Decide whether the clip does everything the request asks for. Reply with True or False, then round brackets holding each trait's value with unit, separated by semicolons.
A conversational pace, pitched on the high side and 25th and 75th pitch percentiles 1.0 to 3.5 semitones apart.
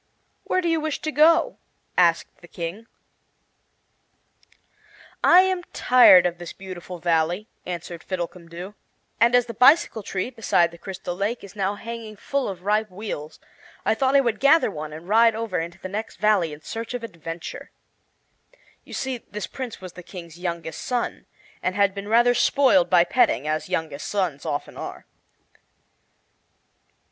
False (160 wpm; 200 Hz; 5.3 semitones)